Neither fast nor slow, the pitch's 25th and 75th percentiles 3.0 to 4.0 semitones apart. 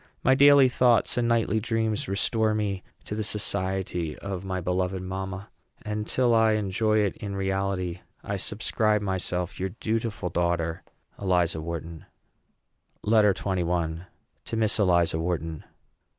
No: slow, 130 wpm; average, 3.3 semitones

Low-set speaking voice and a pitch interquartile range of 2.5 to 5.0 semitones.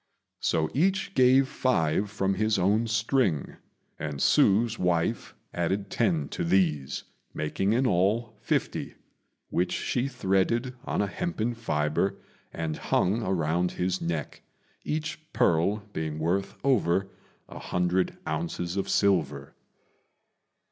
No: very low, 95 Hz; wide, 5.5 semitones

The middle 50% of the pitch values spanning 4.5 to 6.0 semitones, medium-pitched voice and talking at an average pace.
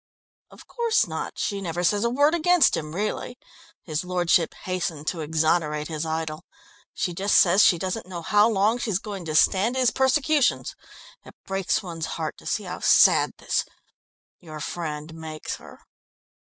Yes: average, 5.2 semitones; medium, 180 Hz; average, 165 wpm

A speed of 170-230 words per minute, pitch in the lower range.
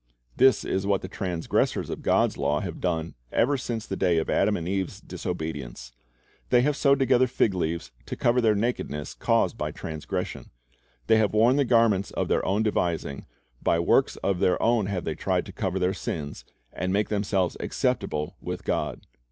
Yes: average, 185 wpm; very low, 95 Hz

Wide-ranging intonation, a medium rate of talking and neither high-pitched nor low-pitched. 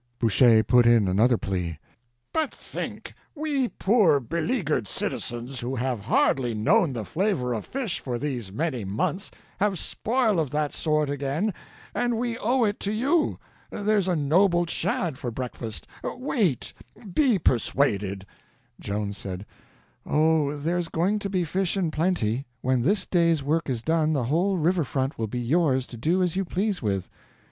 Yes: wide, 7.9 semitones; average, 155 wpm; medium, 155 Hz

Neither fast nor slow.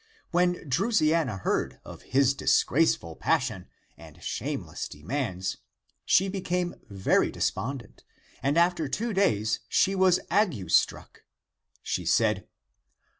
No: slow, 110 wpm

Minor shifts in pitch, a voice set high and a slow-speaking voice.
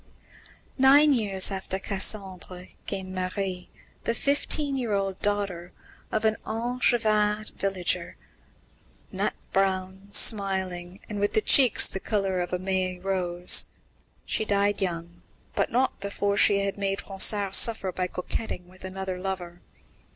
Yes: narrow, 2.2 semitones; high, 195 Hz; slow, 130 wpm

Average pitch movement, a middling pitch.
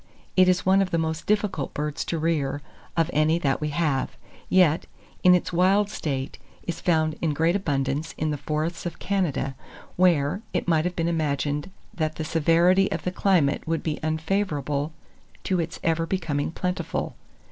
Yes: average, 3.2 semitones; medium, 165 Hz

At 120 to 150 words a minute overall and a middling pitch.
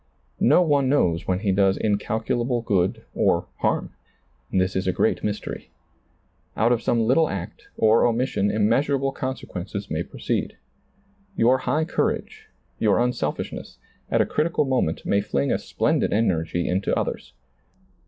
No: average, 145 wpm; low, 110 Hz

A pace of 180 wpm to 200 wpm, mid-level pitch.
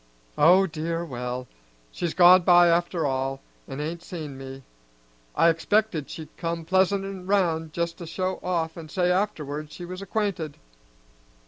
No: average, 145 wpm; medium, 170 Hz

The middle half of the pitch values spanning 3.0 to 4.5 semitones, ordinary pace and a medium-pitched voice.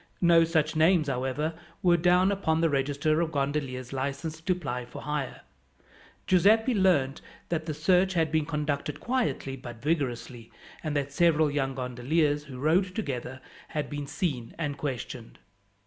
Yes: average, 3.7 semitones; average, 150 wpm; medium, 150 Hz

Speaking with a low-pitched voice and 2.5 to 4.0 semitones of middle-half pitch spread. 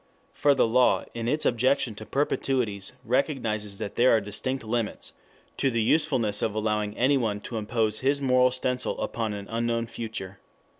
Yes: low, 115 Hz; average, 3.1 semitones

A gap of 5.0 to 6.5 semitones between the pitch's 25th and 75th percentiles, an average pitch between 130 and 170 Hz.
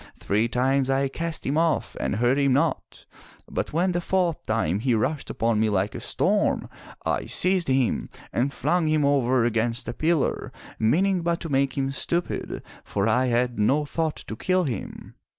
Yes: wide, 5.5 semitones; low, 135 Hz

